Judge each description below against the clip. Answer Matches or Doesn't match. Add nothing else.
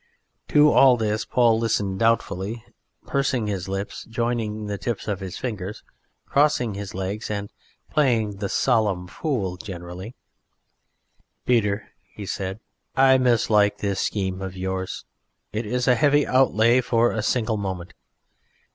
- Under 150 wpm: Matches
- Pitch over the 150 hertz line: Doesn't match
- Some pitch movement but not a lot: Matches